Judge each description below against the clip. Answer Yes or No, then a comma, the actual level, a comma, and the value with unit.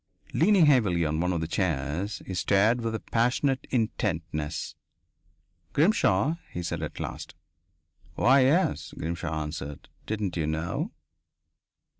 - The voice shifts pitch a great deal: Yes, wide, 7.2 semitones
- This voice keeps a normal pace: No, slow, 125 wpm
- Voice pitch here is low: Yes, very low, 90 Hz